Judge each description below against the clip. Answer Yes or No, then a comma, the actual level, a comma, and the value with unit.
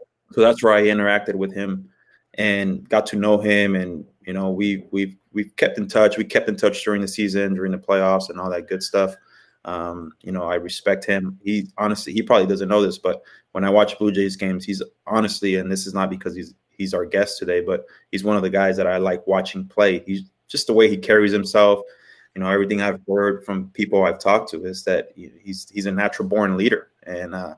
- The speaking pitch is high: No, low, 100 Hz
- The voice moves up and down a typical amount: No, narrow, 1.6 semitones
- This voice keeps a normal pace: No, fast, 235 wpm